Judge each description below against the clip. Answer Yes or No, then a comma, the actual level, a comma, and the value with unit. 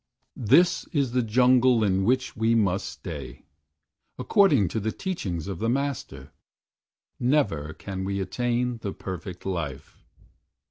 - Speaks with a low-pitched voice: Yes, low, 110 Hz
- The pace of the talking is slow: Yes, slow, 130 wpm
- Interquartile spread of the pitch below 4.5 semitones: No, average, 5.2 semitones